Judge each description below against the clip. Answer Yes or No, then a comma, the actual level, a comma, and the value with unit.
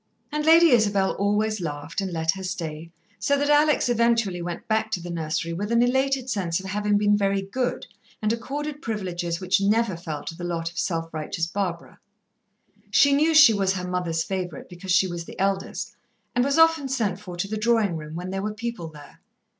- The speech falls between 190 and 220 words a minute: Yes, average, 200 wpm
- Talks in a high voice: Yes, high, 195 Hz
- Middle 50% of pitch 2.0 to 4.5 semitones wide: No, average, 5.3 semitones